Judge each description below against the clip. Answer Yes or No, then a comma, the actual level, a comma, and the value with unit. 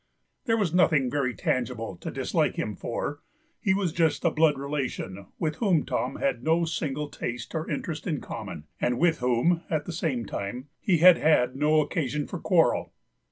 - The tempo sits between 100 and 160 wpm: No, average, 180 wpm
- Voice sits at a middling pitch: Yes, medium, 150 Hz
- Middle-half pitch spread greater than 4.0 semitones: Yes, average, 4.7 semitones